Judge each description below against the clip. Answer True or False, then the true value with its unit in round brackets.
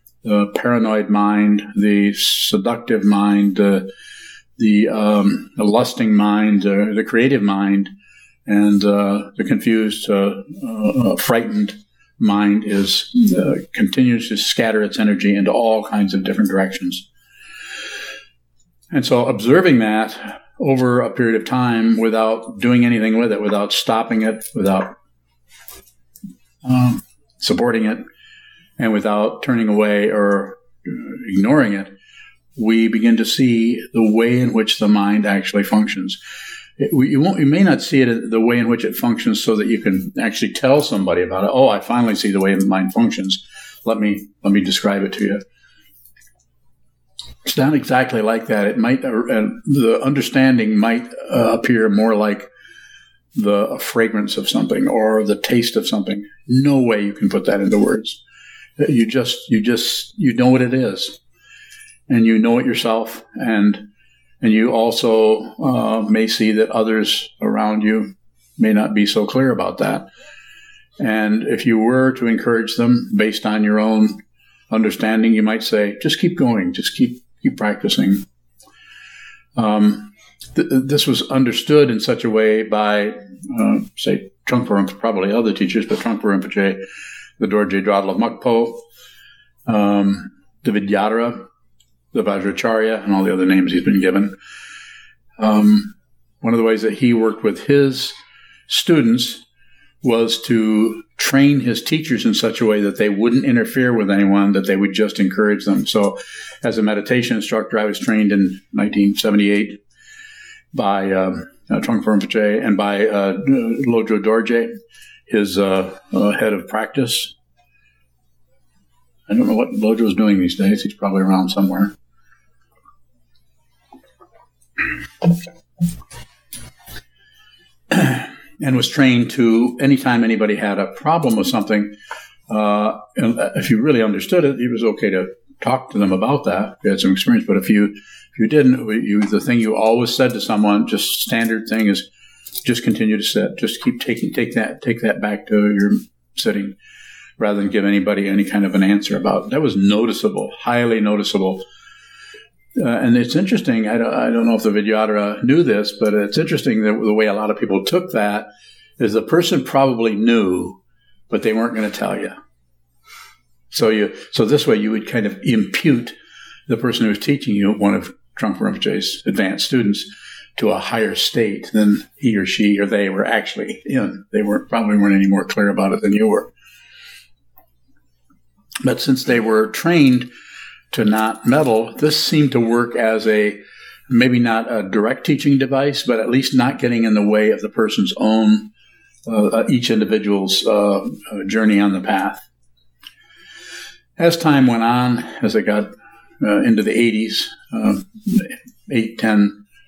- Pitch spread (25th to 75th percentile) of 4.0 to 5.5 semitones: False (3.4 semitones)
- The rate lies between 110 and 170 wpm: True (160 wpm)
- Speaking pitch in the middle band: False (110 Hz)